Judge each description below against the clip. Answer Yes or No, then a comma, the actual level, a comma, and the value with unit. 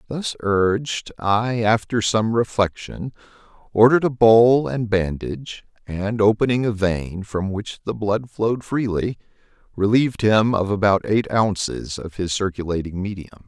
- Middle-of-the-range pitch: No, low, 105 Hz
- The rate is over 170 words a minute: No, average, 140 wpm